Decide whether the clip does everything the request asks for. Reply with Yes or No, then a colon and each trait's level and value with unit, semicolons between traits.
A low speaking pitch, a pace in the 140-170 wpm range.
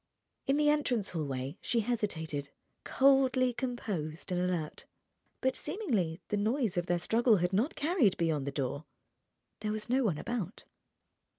No: high, 210 Hz; average, 150 wpm